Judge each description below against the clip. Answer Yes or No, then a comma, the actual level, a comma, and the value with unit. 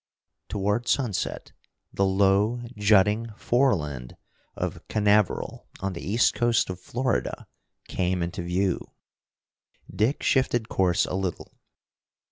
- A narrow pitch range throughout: No, average, 3.8 semitones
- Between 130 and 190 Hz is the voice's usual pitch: No, low, 100 Hz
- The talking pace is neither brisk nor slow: No, slow, 110 wpm